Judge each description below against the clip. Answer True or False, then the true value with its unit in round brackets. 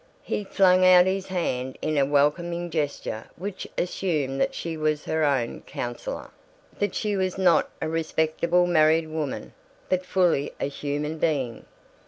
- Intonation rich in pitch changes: False (3.7 semitones)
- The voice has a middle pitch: True (160 Hz)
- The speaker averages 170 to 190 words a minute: False (150 wpm)